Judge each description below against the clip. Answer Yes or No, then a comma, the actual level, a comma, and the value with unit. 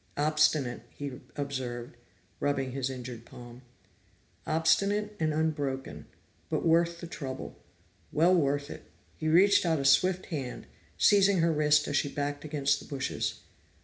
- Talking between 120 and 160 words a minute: Yes, average, 140 wpm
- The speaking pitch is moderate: Yes, medium, 145 Hz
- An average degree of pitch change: Yes, average, 3.4 semitones